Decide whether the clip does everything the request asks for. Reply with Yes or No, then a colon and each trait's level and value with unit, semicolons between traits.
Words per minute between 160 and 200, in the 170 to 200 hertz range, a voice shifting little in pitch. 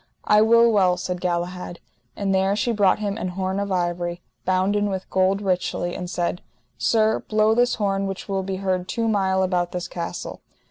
Yes: average, 185 wpm; high, 190 Hz; narrow, 2.2 semitones